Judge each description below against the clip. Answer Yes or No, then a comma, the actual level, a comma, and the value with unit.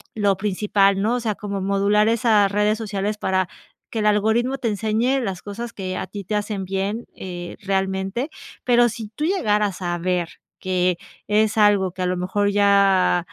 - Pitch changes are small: Yes, narrow, 2.2 semitones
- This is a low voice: No, high, 205 Hz